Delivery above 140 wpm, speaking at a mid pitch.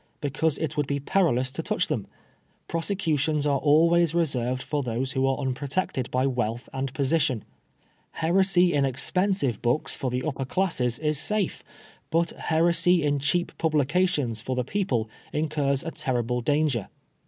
Yes: average, 150 wpm; medium, 145 Hz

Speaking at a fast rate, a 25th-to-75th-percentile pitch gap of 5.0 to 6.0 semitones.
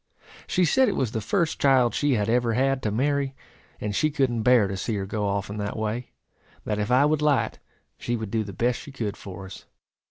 No: fast, 230 wpm; average, 4.5 semitones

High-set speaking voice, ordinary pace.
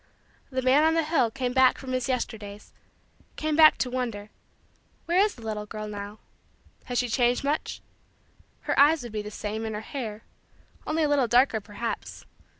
Yes: high, 245 Hz; average, 180 wpm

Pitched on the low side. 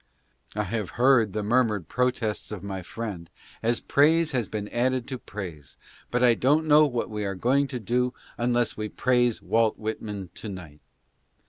Yes: low, 115 Hz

